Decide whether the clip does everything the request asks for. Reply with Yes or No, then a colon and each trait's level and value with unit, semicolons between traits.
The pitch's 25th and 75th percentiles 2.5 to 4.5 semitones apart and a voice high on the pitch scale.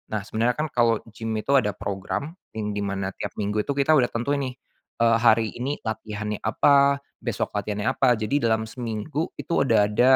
No: average, 4.2 semitones; low, 115 Hz